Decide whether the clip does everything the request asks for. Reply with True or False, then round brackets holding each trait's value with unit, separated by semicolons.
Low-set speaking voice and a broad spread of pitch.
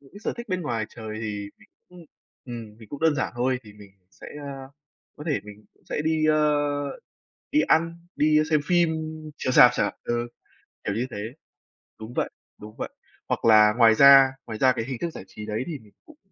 True (125 Hz; 6.0 semitones)